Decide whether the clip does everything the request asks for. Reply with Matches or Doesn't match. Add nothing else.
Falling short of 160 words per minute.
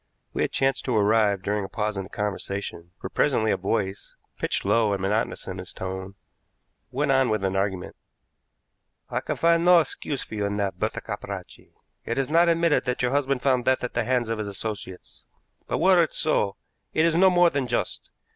Doesn't match